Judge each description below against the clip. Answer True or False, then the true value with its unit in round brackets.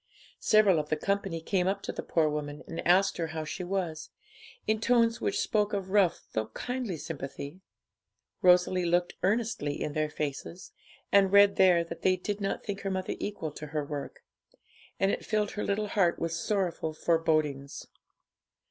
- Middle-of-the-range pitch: True (180 Hz)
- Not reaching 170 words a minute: False (175 wpm)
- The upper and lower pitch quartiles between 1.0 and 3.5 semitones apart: False (4.2 semitones)